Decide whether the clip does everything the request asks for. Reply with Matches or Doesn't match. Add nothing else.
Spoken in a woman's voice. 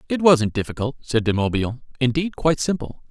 Doesn't match